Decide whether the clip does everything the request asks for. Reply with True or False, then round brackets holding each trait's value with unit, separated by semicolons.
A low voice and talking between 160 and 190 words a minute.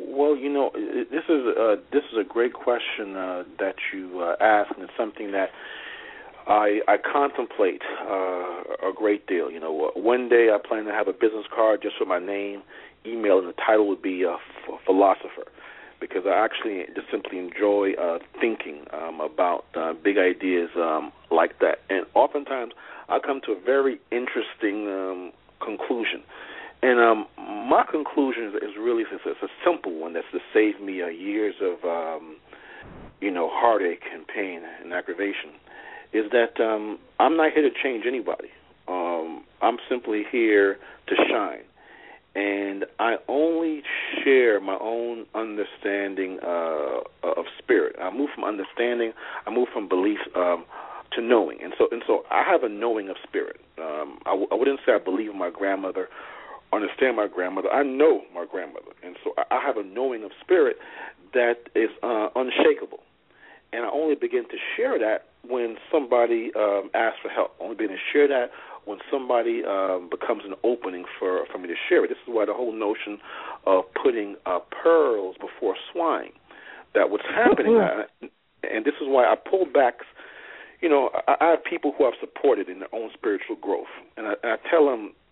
False (145 Hz; 175 wpm)